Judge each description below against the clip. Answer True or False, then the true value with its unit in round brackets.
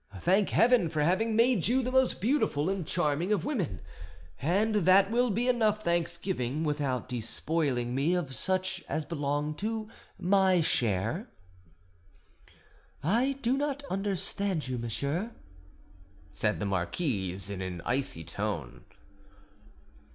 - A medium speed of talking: False (125 wpm)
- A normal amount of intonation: False (8.2 semitones)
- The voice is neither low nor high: True (175 Hz)